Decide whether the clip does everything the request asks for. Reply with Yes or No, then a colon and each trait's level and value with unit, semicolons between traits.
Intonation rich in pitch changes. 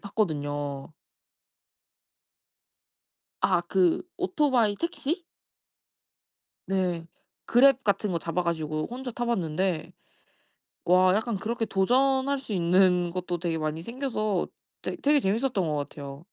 Yes: wide, 6.4 semitones